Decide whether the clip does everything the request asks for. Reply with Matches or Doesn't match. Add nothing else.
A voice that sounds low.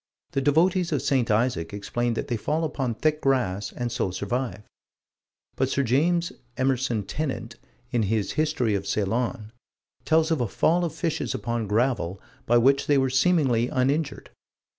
Matches